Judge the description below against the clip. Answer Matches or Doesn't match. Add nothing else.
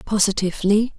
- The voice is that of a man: Doesn't match